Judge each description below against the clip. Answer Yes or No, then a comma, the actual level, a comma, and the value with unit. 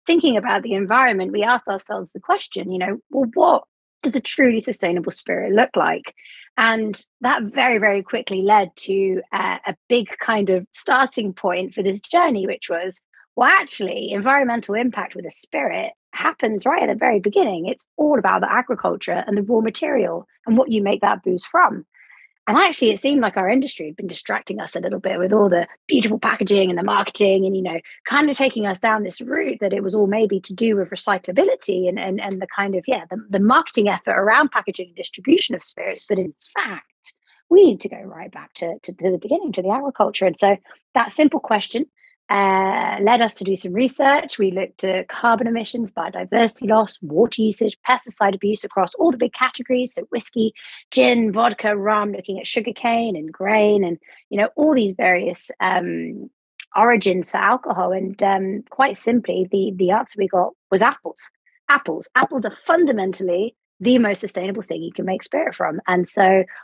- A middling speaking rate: Yes, average, 195 wpm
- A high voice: Yes, high, 210 Hz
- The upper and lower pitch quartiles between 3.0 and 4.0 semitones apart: No, average, 4.7 semitones